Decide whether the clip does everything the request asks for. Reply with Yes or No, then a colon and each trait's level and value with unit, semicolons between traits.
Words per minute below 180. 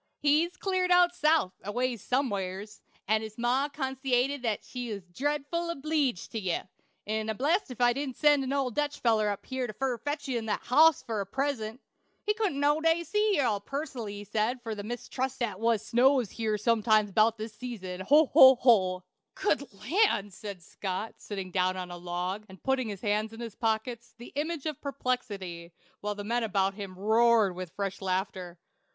No: average, 190 wpm